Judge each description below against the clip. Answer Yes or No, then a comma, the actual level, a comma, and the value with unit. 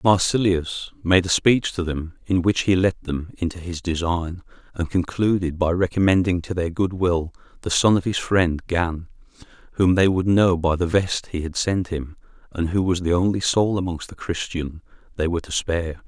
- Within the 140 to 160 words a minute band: No, average, 195 wpm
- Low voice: Yes, very low, 90 Hz